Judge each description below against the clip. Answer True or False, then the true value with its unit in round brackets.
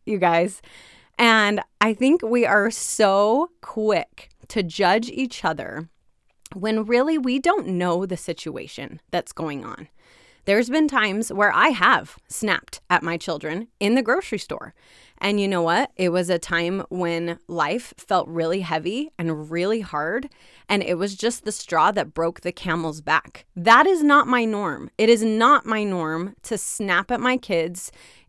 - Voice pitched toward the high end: True (205 Hz)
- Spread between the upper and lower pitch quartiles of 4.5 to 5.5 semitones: True (5.0 semitones)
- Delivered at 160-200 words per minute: True (170 wpm)